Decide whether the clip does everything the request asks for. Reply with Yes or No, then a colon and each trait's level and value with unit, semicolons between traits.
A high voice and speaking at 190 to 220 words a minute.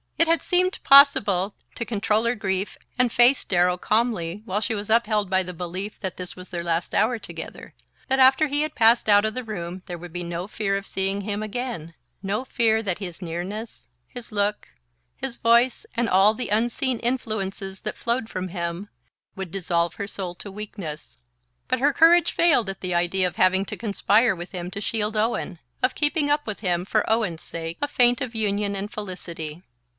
Yes: high, 205 Hz; average, 195 wpm